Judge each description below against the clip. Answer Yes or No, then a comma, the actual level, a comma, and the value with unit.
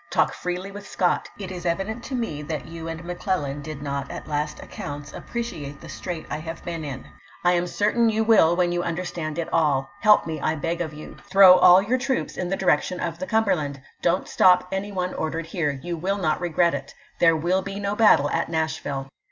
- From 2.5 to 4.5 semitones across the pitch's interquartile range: Yes, average, 3.6 semitones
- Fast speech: Yes, fast, 220 wpm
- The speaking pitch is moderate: Yes, medium, 175 Hz